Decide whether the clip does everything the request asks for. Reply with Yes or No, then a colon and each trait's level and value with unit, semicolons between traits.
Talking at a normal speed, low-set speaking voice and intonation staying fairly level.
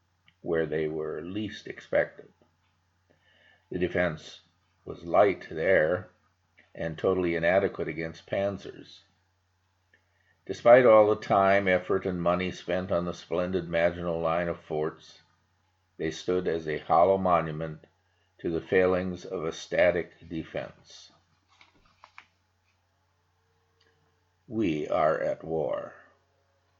No: slow, 105 wpm; very low, 90 Hz; narrow, 1.7 semitones